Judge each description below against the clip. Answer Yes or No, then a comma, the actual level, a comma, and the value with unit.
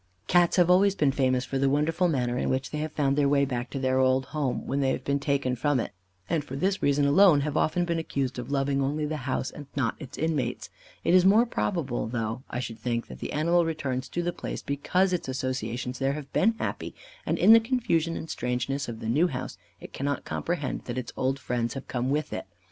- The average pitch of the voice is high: No, medium, 140 Hz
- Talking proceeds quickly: Yes, fast, 235 wpm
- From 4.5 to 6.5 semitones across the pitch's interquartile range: No, average, 3.9 semitones